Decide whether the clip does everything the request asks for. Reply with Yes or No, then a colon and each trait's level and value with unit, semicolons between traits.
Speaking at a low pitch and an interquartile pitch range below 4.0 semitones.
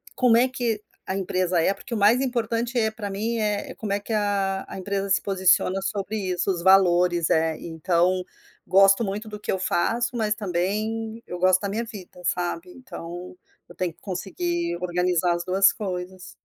No: high, 195 Hz; average, 3.2 semitones